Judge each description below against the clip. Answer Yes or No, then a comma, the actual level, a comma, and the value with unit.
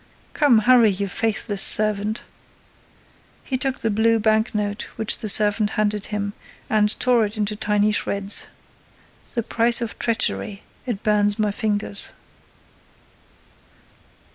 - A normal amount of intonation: No, narrow, 1.7 semitones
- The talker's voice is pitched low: No, high, 215 Hz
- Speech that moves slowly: Yes, slow, 125 wpm